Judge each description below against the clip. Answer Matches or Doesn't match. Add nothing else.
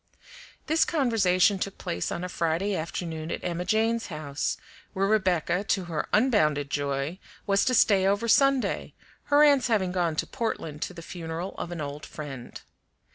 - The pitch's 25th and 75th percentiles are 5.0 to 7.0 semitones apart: Matches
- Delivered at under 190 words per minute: Matches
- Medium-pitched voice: Matches